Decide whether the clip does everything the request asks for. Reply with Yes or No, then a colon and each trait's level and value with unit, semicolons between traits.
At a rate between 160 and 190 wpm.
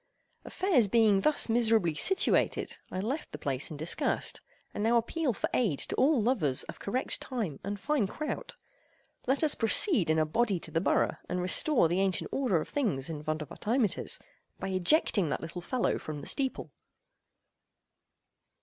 Yes: average, 165 wpm